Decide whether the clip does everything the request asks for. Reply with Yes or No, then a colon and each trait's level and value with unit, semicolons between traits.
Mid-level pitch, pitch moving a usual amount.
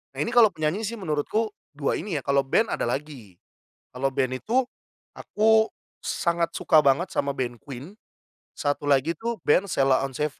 No: medium, 150 Hz; wide, 6.7 semitones